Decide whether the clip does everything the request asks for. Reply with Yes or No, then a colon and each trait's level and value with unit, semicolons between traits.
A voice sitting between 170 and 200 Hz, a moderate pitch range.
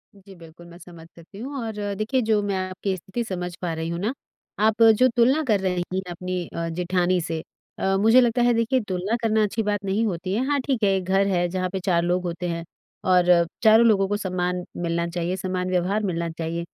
Yes: medium, 185 Hz; average, 3.6 semitones